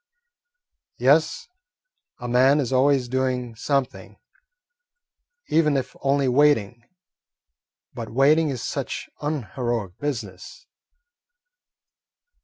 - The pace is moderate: No, slow, 80 wpm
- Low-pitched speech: Yes, low, 130 Hz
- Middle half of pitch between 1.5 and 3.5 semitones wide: Yes, average, 3.0 semitones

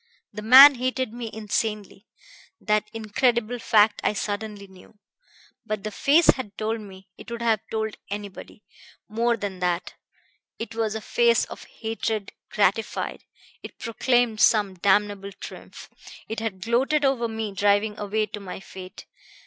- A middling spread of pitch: No, narrow, 2.2 semitones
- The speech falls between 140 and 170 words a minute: Yes, average, 145 wpm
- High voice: Yes, high, 215 Hz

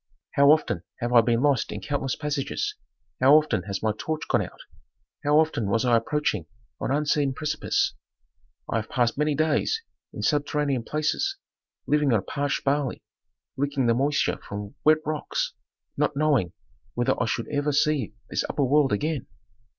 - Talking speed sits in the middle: Yes, average, 160 wpm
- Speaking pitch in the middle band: Yes, medium, 145 Hz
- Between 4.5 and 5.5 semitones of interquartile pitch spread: No, average, 4.0 semitones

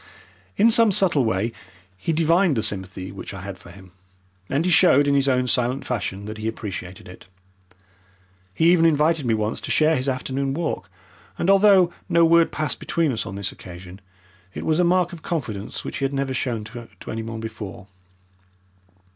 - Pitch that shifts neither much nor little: No, wide, 7.8 semitones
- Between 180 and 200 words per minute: Yes, average, 185 wpm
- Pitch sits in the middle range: No, low, 130 Hz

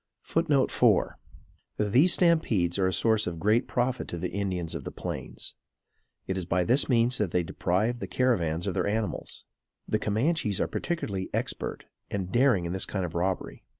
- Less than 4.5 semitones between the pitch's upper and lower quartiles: No, average, 5.2 semitones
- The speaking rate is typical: Yes, average, 175 wpm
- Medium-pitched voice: No, low, 105 Hz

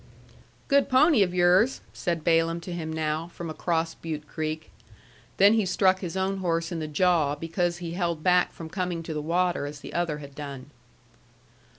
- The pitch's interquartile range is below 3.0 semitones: Yes, narrow, 2.4 semitones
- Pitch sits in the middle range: Yes, medium, 170 Hz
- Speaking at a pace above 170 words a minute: Yes, average, 185 wpm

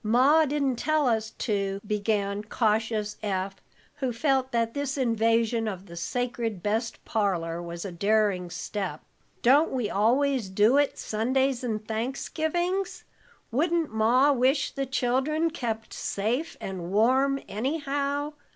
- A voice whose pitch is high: Yes, high, 230 Hz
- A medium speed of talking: No, slow, 130 wpm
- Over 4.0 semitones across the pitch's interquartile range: Yes, average, 4.7 semitones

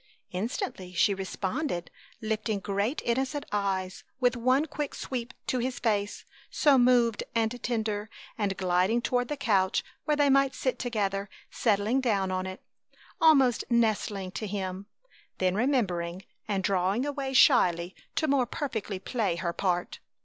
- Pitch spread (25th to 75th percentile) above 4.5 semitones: Yes, average, 5.0 semitones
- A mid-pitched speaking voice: No, high, 220 Hz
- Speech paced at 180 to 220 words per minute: No, average, 140 wpm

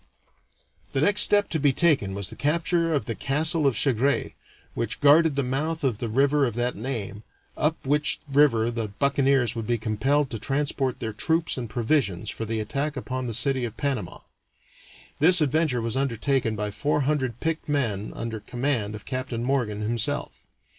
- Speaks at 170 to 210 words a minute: Yes, average, 175 wpm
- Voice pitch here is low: Yes, low, 130 Hz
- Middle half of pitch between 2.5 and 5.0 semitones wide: Yes, average, 4.3 semitones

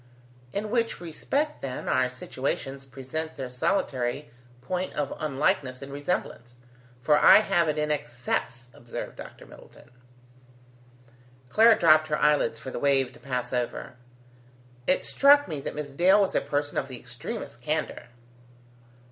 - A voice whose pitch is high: No, medium, 145 Hz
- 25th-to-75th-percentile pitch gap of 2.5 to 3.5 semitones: No, average, 5.0 semitones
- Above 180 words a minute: No, average, 145 wpm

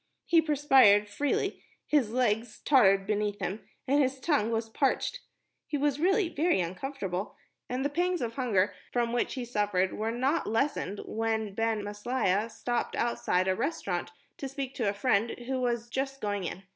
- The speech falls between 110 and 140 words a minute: No, average, 170 wpm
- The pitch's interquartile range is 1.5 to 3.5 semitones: No, average, 4.7 semitones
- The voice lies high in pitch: Yes, high, 235 Hz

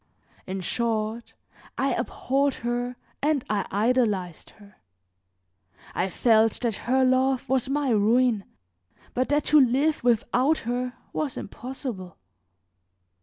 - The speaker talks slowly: Yes, slow, 115 wpm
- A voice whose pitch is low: No, high, 245 Hz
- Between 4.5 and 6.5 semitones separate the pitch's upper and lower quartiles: No, average, 3.3 semitones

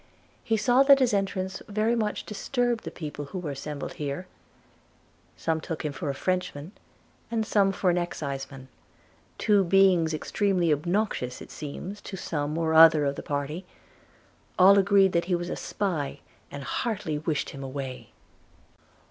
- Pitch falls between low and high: Yes, medium, 175 Hz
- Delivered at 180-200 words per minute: No, average, 155 wpm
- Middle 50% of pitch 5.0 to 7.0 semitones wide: Yes, average, 5.3 semitones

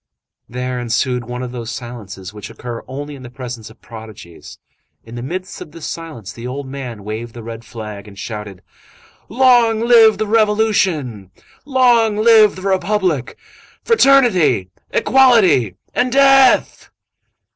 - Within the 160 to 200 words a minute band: No, average, 140 wpm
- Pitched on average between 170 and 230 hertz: No, low, 130 Hz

